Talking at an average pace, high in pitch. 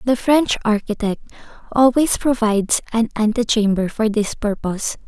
No: slow, 120 wpm; high, 225 Hz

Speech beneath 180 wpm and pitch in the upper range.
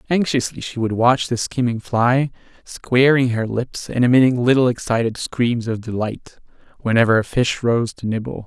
No: average, 165 wpm; low, 120 Hz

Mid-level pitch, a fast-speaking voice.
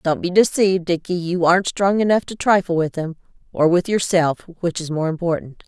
No: medium, 175 Hz; average, 190 wpm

